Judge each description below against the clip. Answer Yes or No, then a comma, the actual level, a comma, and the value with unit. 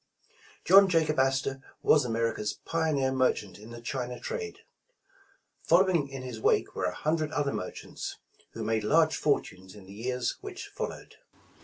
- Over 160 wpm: No, average, 155 wpm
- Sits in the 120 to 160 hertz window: Yes, low, 135 Hz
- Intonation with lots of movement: Yes, wide, 5.7 semitones